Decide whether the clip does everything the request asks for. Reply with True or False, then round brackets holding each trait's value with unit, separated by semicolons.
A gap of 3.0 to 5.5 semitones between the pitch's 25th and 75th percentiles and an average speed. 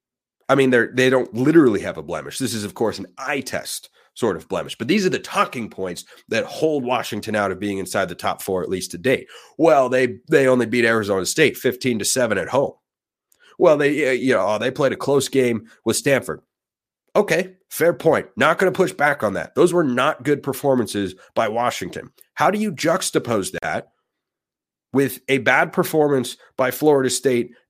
True (3.7 semitones; 195 wpm)